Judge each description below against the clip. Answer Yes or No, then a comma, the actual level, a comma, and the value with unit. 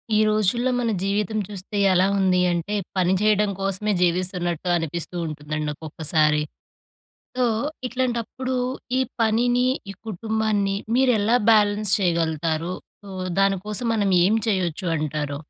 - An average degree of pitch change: Yes, average, 4.2 semitones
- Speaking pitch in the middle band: No, high, 195 Hz